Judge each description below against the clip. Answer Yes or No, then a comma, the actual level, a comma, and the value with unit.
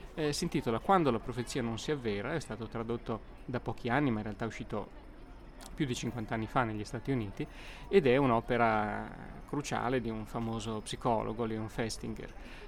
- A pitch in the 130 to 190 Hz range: No, low, 115 Hz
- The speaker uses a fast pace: Yes, fast, 180 wpm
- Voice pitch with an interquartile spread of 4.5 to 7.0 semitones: No, average, 2.9 semitones